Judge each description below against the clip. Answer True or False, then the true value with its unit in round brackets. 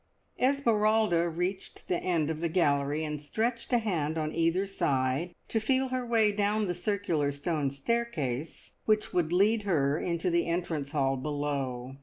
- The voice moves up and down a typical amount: False (6.2 semitones)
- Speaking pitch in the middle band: True (170 Hz)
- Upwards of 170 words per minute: False (160 wpm)